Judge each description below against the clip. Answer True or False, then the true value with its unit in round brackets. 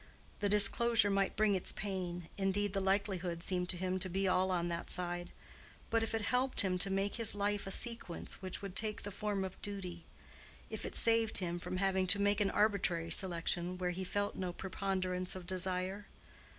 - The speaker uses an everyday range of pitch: False (2.1 semitones)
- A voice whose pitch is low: False (190 Hz)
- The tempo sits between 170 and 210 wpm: True (190 wpm)